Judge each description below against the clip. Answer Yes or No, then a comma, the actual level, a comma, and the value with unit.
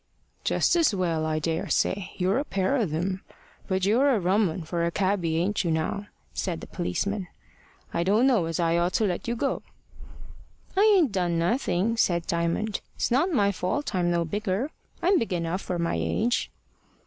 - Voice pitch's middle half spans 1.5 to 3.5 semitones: No, average, 4.3 semitones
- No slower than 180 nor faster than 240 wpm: Yes, average, 190 wpm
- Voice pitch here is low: No, medium, 185 Hz